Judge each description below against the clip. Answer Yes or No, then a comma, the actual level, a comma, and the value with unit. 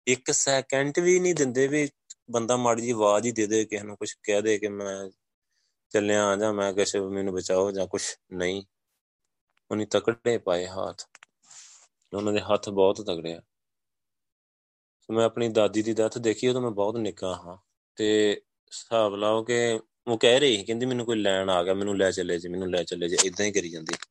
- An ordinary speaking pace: No, fast, 190 wpm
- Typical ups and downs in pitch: Yes, average, 3.2 semitones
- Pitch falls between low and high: No, low, 105 Hz